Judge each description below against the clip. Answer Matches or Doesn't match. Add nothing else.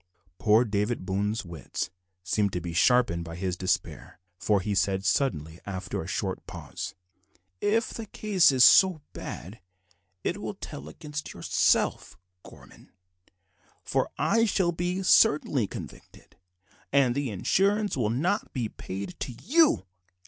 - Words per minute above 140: Doesn't match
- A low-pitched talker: Matches